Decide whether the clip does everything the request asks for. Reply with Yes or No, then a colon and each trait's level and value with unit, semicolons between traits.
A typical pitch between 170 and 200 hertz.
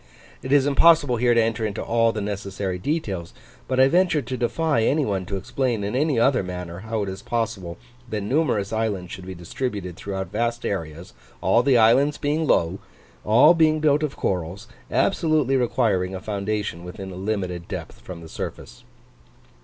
No: low, 110 Hz